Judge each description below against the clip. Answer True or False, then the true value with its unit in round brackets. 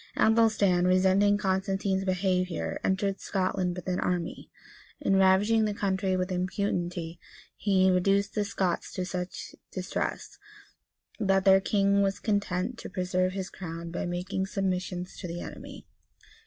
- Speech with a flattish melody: True (1.5 semitones)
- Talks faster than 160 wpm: False (135 wpm)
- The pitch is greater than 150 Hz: True (190 Hz)